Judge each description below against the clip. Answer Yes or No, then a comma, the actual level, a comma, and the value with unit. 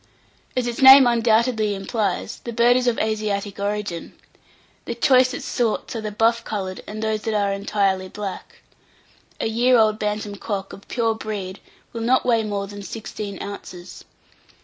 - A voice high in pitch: Yes, high, 215 Hz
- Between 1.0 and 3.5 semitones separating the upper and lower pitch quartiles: Yes, narrow, 2.6 semitones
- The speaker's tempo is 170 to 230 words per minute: No, average, 160 wpm